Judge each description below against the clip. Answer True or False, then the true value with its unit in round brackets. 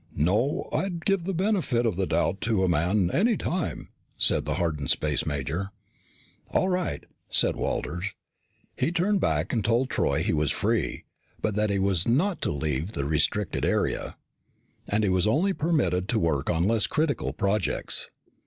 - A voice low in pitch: True (105 Hz)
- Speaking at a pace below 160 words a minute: False (170 wpm)